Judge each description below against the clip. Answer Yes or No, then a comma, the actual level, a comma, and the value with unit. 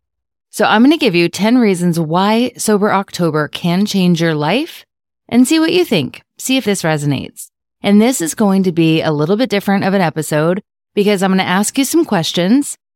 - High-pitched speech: Yes, high, 195 Hz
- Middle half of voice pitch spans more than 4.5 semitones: Yes, average, 5.2 semitones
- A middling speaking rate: No, fast, 210 wpm